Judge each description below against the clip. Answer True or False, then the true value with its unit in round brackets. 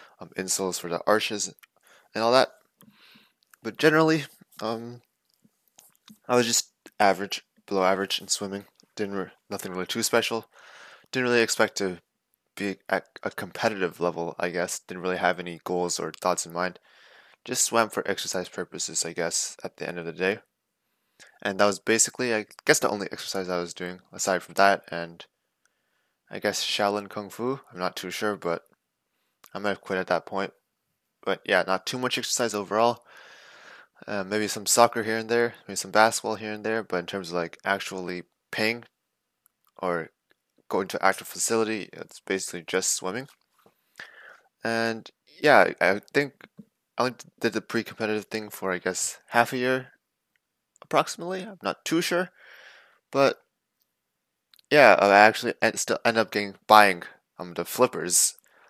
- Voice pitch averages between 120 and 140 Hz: False (105 Hz)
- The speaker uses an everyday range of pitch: True (4.0 semitones)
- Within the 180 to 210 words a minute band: False (165 wpm)